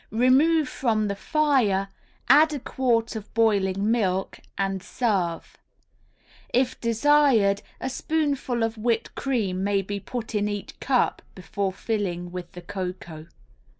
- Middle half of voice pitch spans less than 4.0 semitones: No, average, 4.8 semitones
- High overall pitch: Yes, high, 215 Hz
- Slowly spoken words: Yes, slow, 130 wpm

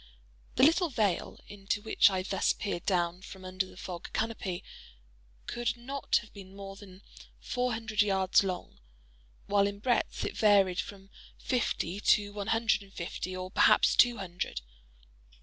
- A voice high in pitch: Yes, high, 200 Hz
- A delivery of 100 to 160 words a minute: Yes, average, 155 wpm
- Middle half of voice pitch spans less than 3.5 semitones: Yes, average, 2.9 semitones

